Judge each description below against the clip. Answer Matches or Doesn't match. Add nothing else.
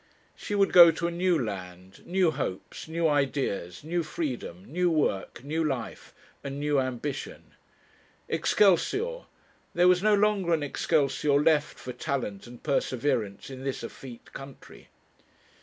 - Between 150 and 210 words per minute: Doesn't match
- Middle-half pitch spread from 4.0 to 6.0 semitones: Matches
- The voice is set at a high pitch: Doesn't match